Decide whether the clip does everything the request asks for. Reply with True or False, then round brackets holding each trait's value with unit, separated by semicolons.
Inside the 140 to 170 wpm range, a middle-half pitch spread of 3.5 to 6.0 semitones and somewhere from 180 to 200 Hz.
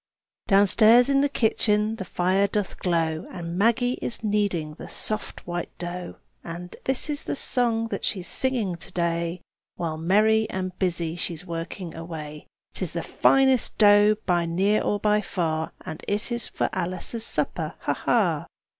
True (165 wpm; 4.3 semitones; 190 Hz)